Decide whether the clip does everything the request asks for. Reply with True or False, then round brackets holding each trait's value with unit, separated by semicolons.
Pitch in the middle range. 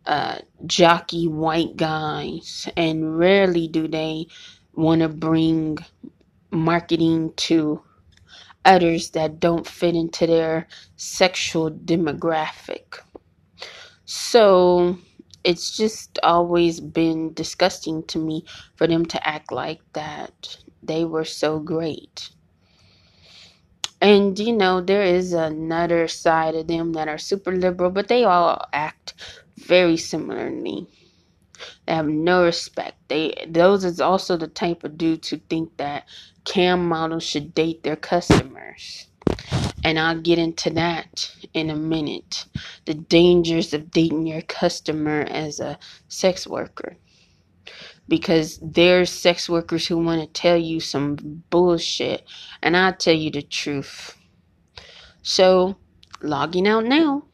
True (165 Hz)